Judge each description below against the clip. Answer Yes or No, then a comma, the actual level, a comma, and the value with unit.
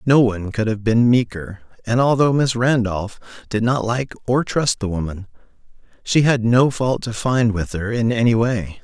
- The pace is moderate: Yes, average, 190 wpm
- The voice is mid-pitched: No, low, 115 Hz